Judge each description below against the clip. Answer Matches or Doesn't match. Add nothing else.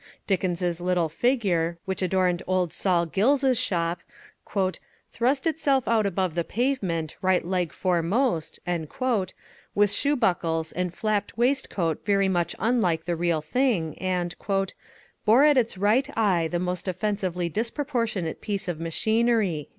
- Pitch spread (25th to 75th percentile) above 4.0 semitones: Matches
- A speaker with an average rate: Doesn't match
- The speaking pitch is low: Doesn't match